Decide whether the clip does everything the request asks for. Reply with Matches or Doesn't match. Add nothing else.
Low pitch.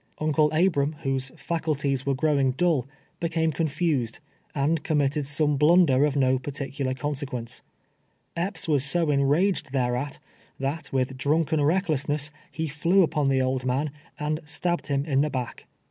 Doesn't match